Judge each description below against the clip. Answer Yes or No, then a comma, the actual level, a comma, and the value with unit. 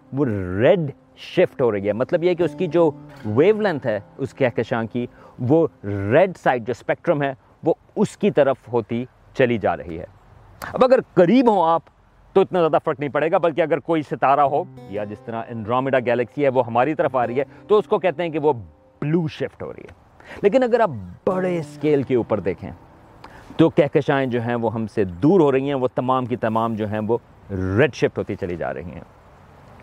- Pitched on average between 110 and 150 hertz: Yes, low, 135 Hz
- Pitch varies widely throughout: Yes, wide, 5.9 semitones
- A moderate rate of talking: No, fast, 215 wpm